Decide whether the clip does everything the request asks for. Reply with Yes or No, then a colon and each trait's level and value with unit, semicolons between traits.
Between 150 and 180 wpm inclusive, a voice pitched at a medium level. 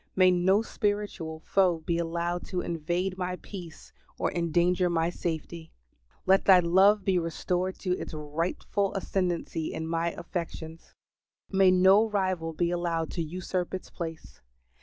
No: average, 140 wpm; medium, 175 Hz